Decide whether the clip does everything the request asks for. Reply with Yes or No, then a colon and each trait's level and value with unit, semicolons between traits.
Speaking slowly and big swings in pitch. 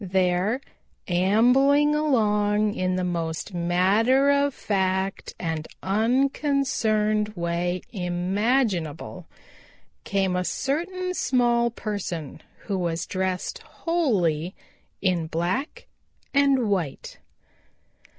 Yes: slow, 85 wpm; wide, 6.2 semitones